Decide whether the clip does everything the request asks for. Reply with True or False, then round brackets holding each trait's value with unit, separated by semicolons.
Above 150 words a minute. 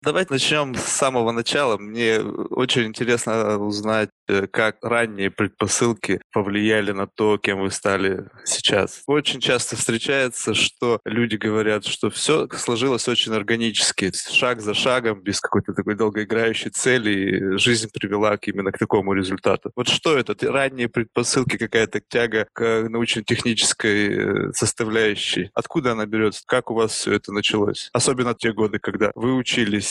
False (145 wpm)